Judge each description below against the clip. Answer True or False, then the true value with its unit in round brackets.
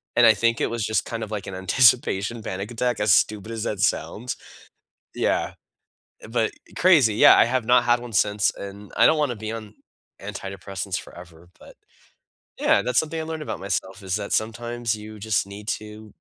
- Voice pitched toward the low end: True (110 Hz)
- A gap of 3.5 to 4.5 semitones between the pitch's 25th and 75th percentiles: False (3.1 semitones)